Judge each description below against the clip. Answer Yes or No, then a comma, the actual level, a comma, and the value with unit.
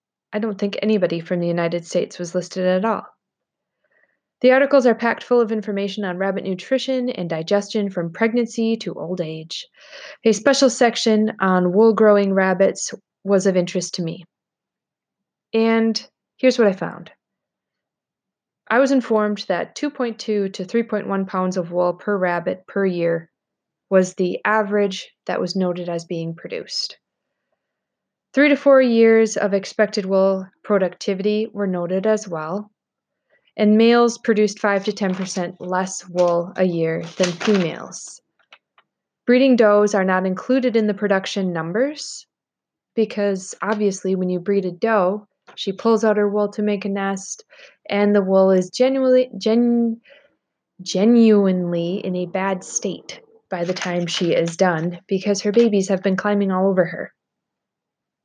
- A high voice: Yes, high, 200 Hz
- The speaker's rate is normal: Yes, average, 150 wpm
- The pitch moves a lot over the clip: No, average, 3.4 semitones